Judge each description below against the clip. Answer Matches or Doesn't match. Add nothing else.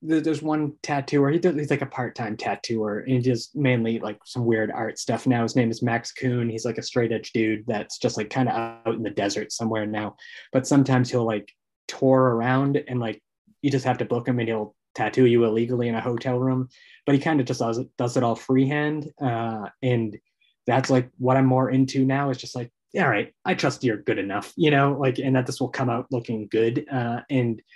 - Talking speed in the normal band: Doesn't match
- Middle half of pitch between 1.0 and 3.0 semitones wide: Matches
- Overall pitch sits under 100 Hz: Doesn't match